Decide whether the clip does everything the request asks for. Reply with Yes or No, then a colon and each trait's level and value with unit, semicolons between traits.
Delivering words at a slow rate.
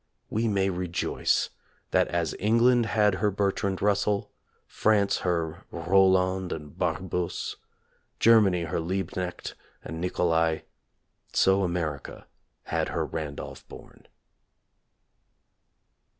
Yes: slow, 105 wpm